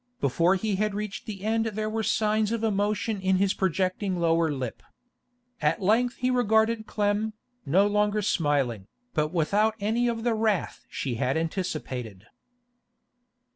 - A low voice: No, high, 205 Hz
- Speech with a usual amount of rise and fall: Yes, average, 4.8 semitones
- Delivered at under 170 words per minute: Yes, average, 145 wpm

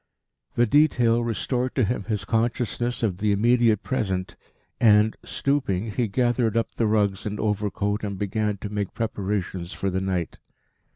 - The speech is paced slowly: No, average, 155 wpm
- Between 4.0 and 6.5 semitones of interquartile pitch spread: No, average, 2.9 semitones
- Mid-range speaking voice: No, low, 105 Hz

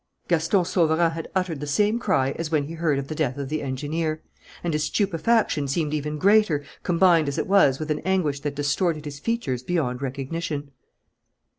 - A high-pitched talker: No, medium, 155 Hz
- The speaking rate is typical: Yes, average, 185 wpm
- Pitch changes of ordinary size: Yes, average, 3.3 semitones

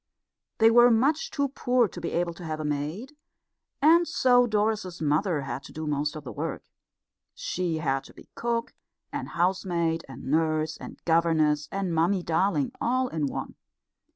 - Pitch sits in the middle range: Yes, medium, 170 Hz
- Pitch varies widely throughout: Yes, wide, 6.6 semitones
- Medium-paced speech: Yes, average, 170 wpm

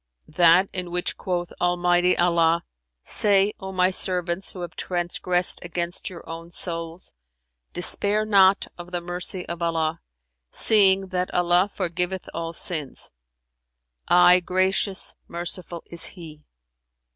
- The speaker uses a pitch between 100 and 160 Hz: No, medium, 175 Hz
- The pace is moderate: No, slow, 120 wpm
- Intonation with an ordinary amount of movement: No, narrow, 1.4 semitones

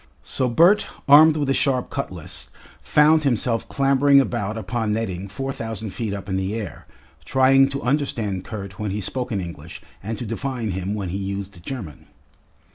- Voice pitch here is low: Yes, low, 115 Hz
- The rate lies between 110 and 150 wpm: No, average, 175 wpm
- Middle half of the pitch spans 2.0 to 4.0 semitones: No, wide, 5.4 semitones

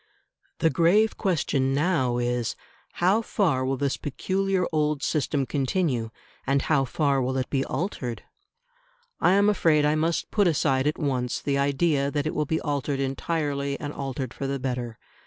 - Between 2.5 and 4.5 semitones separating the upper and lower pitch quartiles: Yes, average, 3.5 semitones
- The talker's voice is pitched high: No, medium, 140 Hz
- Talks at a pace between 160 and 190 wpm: Yes, average, 165 wpm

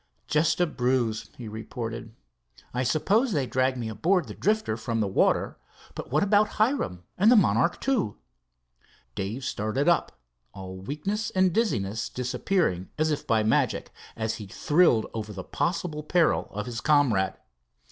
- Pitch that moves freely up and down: Yes, wide, 8.2 semitones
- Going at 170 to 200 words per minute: No, average, 155 wpm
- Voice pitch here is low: Yes, low, 130 Hz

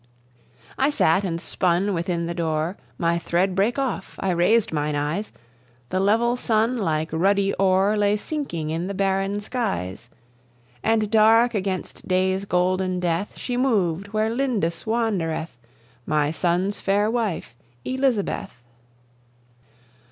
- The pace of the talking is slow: Yes, slow, 130 wpm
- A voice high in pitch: Yes, high, 195 Hz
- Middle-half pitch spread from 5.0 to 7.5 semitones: No, average, 4.3 semitones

